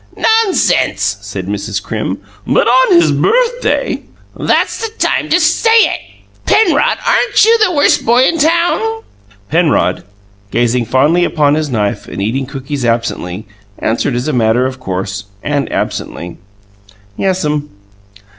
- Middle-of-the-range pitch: Yes, medium, 145 Hz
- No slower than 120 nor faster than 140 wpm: Yes, slow, 135 wpm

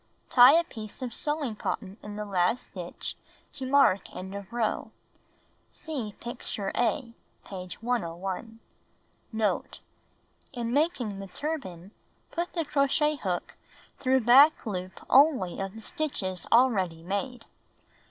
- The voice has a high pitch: Yes, high, 230 Hz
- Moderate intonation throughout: No, wide, 5.8 semitones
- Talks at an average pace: No, slow, 130 wpm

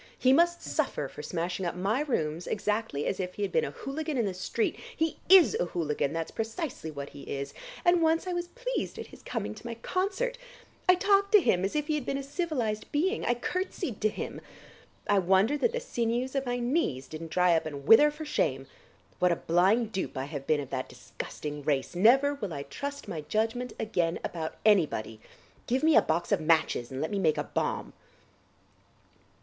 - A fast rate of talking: Yes, fast, 210 wpm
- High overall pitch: Yes, high, 220 Hz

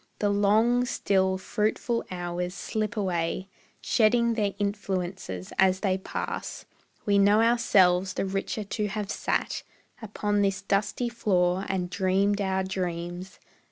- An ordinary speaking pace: No, slow, 125 wpm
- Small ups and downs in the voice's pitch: Yes, narrow, 2.1 semitones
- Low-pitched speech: No, high, 195 Hz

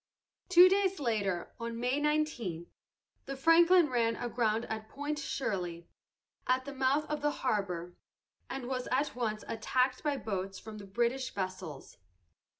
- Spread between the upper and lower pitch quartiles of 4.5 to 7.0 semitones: Yes, average, 5.3 semitones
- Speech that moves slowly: No, average, 145 wpm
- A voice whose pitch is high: Yes, high, 245 Hz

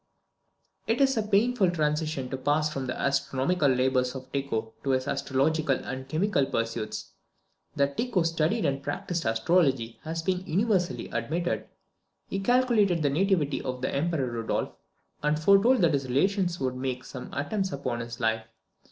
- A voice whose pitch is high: No, medium, 145 Hz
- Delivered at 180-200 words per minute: No, average, 155 wpm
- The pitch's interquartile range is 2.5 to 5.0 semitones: No, wide, 5.5 semitones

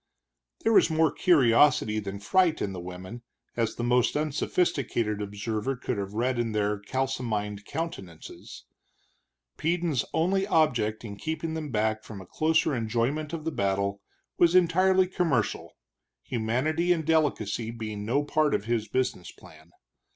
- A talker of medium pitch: No, low, 120 Hz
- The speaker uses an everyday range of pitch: No, wide, 7.0 semitones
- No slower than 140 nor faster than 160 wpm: Yes, average, 145 wpm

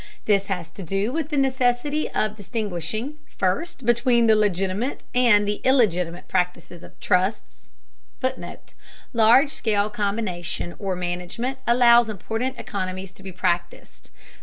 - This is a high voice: Yes, high, 210 Hz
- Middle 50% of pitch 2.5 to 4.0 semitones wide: No, average, 4.9 semitones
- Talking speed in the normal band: No, slow, 130 wpm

